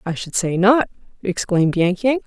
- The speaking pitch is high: Yes, high, 200 Hz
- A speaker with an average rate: Yes, average, 185 wpm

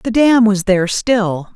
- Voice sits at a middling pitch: No, high, 210 Hz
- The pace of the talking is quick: No, average, 195 wpm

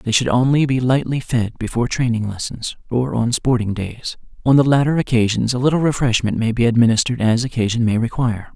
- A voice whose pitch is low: Yes, low, 120 Hz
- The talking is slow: No, average, 190 wpm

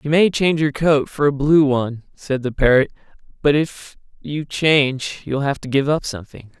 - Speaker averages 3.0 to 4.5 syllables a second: No, 5.1 syllables/s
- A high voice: No, medium, 140 Hz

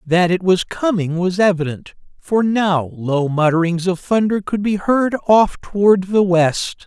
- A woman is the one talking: No, male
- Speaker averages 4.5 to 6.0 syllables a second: No, 4.1 syllables/s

